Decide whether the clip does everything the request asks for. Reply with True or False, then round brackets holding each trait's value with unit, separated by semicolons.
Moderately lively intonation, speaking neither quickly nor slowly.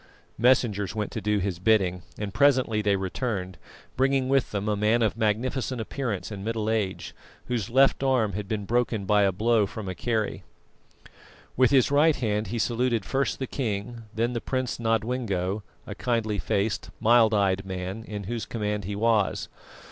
True (3.1 semitones; 170 wpm)